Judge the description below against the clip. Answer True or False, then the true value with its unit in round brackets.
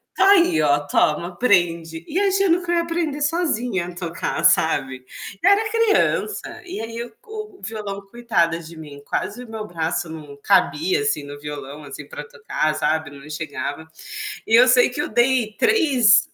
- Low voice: False (210 Hz)